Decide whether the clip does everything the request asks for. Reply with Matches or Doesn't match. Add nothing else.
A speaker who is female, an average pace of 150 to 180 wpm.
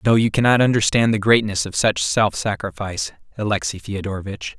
Doesn't match